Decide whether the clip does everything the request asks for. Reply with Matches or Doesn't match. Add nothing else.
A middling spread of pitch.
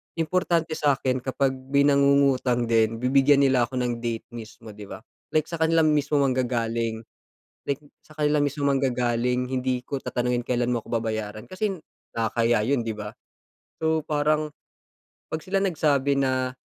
Matches